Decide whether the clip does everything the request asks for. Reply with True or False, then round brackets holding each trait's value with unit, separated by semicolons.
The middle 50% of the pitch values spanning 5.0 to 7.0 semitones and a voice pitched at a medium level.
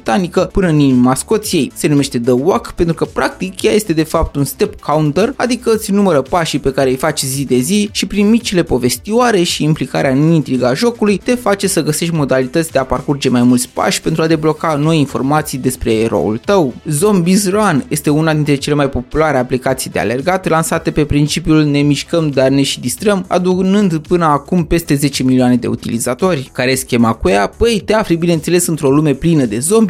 True (5.6 semitones; 155 Hz)